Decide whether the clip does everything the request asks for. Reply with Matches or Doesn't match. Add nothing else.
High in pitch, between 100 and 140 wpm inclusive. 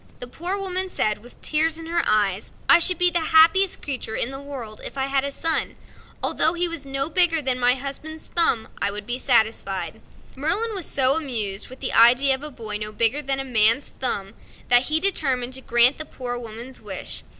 Doesn't match